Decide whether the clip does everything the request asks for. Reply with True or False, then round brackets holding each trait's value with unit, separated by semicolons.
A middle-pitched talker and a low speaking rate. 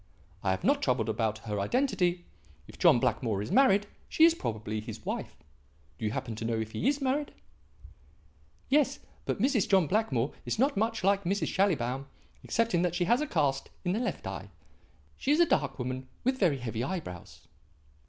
False (175 Hz; 185 wpm)